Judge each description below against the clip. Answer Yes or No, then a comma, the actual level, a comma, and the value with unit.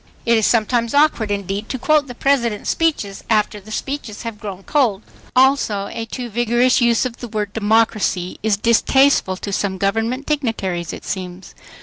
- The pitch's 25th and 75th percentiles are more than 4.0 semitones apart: No, average, 3.7 semitones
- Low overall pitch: No, high, 225 Hz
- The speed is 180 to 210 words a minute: No, average, 165 wpm